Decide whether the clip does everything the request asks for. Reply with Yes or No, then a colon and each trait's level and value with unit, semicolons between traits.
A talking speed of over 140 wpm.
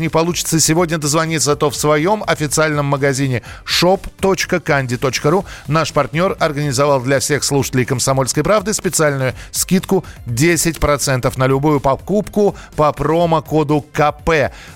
No: slow, 110 wpm